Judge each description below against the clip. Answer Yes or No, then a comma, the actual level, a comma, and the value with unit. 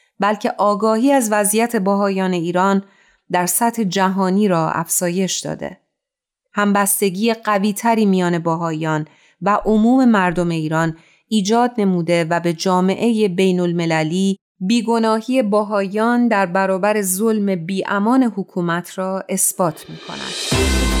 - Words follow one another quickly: No, average, 110 wpm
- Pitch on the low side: No, high, 195 Hz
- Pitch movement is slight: No, average, 3.3 semitones